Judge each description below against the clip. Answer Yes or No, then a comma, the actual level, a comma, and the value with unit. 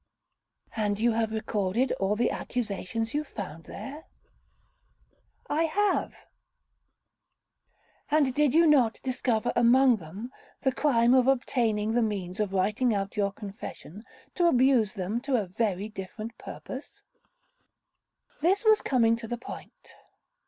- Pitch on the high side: Yes, high, 230 Hz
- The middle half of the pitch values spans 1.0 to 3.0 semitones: No, average, 4.2 semitones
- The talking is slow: Yes, slow, 125 wpm